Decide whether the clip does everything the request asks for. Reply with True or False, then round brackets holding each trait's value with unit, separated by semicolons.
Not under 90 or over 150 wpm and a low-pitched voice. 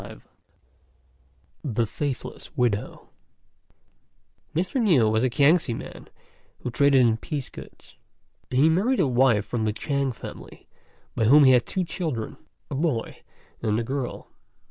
True (140 wpm; 130 Hz)